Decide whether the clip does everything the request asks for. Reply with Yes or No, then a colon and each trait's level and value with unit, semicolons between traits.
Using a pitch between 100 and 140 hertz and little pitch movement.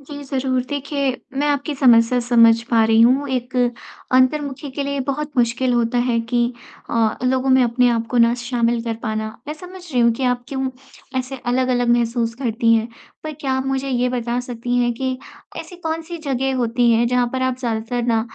No: very high, 250 Hz; narrow, 2.3 semitones